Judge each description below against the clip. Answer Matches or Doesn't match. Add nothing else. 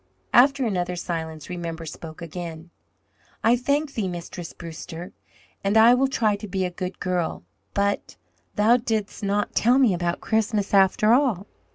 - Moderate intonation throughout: Matches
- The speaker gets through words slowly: Doesn't match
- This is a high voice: Matches